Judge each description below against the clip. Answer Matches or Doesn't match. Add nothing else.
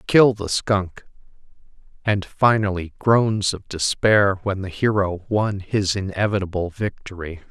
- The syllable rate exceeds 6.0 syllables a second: Doesn't match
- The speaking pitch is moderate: Doesn't match